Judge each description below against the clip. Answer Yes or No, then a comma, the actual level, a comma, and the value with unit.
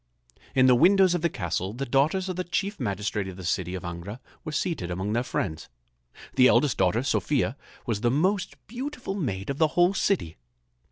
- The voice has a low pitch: Yes, low, 130 Hz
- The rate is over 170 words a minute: Yes, average, 190 wpm